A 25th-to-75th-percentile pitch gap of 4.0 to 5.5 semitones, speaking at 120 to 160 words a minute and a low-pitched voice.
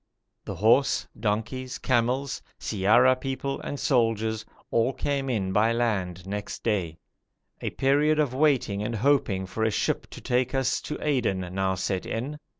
Yes: average, 4.4 semitones; average, 150 wpm; low, 115 Hz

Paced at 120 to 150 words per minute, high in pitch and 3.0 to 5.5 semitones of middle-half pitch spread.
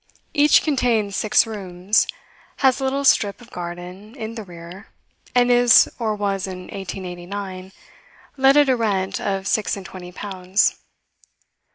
Yes: average, 145 wpm; high, 205 Hz; average, 4.6 semitones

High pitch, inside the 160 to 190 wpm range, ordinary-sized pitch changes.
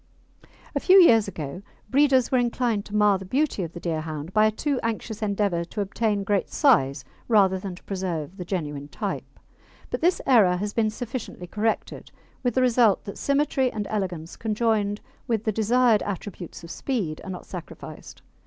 Yes: high, 210 Hz; average, 175 wpm; average, 4.6 semitones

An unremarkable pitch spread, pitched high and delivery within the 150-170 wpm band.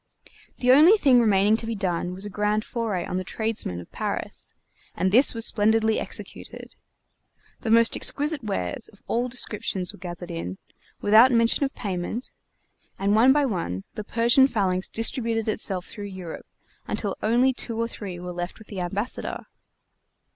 Yes: average, 3.9 semitones; high, 215 Hz; average, 165 wpm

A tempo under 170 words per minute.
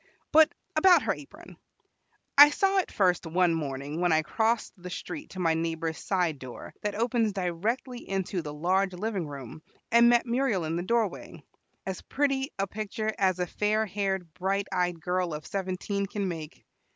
No: average, 175 wpm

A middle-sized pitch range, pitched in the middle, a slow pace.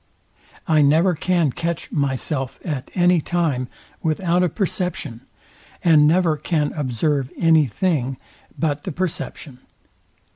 Yes: average, 3.7 semitones; medium, 155 Hz; slow, 115 wpm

